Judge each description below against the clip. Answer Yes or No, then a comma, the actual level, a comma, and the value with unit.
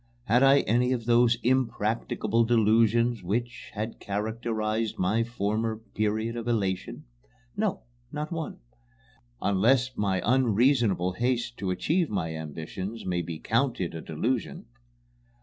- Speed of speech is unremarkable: No, slow, 120 wpm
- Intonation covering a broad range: No, average, 3.1 semitones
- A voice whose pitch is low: Yes, low, 115 Hz